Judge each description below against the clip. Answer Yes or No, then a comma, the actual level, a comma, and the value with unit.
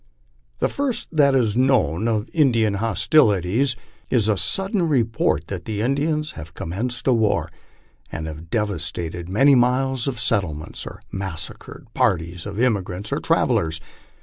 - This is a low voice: Yes, low, 110 Hz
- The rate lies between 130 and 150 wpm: Yes, average, 145 wpm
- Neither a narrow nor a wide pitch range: No, wide, 6.7 semitones